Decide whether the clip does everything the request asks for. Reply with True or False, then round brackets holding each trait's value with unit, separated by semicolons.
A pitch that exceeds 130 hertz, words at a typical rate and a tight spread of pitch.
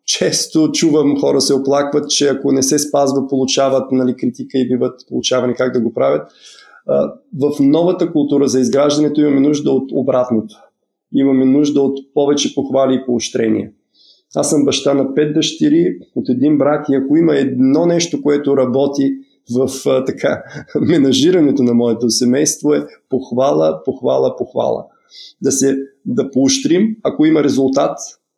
True (140 Hz; 145 wpm; 2.0 semitones)